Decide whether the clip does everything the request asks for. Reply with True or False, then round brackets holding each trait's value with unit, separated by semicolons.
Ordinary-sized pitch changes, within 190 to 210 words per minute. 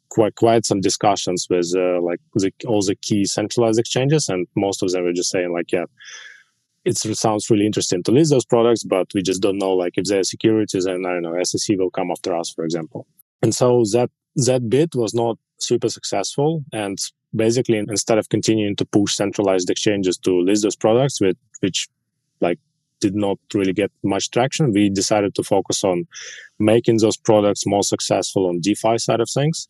True (3.8 semitones; 195 wpm)